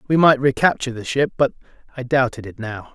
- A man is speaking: Yes, male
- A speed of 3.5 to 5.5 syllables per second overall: No, 6.1 syllables/s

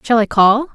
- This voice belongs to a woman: Yes, female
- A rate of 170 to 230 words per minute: No, fast, 240 wpm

